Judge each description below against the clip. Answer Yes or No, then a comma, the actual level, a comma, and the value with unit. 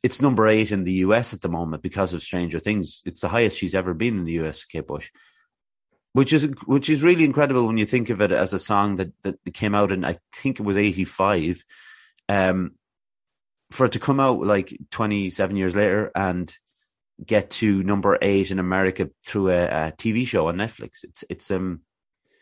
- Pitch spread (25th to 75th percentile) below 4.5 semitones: Yes, average, 3.5 semitones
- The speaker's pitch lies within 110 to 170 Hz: No, low, 100 Hz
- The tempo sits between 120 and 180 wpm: No, fast, 205 wpm